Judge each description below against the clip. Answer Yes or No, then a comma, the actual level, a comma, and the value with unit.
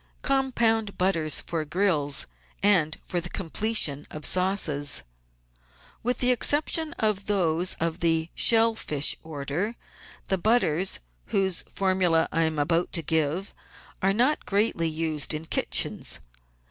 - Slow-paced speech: Yes, slow, 130 wpm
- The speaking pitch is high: No, medium, 180 Hz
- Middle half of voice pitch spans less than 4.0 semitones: No, average, 4.8 semitones